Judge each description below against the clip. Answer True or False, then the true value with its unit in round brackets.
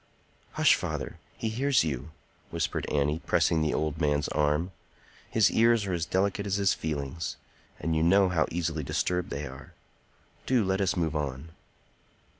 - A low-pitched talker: True (80 Hz)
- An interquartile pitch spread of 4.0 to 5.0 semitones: True (4.3 semitones)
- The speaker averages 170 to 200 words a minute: False (160 wpm)